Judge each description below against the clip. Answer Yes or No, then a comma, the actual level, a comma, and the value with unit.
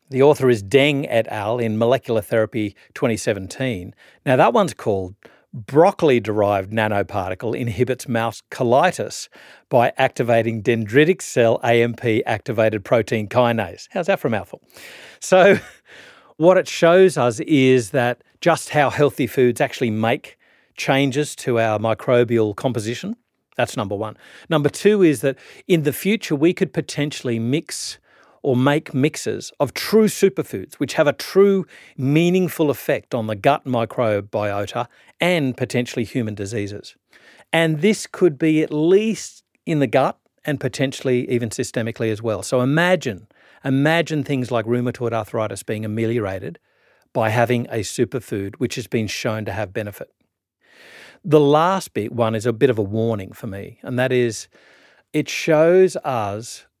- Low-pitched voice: Yes, low, 125 Hz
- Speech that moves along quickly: No, average, 145 wpm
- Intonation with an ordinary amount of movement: Yes, average, 4.9 semitones